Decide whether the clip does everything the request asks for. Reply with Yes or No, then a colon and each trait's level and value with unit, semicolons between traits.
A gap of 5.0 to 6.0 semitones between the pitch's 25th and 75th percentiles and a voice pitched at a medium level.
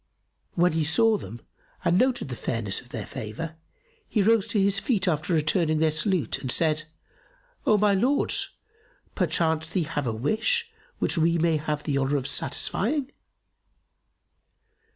Yes: average, 5.3 semitones; medium, 160 Hz